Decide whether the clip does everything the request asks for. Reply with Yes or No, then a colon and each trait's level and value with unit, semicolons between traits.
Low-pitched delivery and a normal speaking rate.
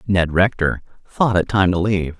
Yes: very low, 95 Hz; average, 190 wpm